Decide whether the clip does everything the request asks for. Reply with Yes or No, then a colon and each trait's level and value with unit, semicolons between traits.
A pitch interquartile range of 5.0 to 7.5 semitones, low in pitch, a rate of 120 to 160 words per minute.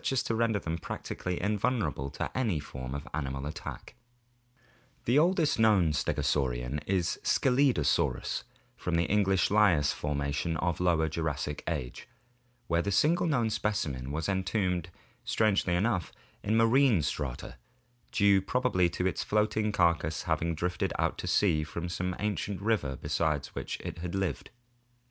Yes: wide, 5.6 semitones; very low, 90 Hz; slow, 135 wpm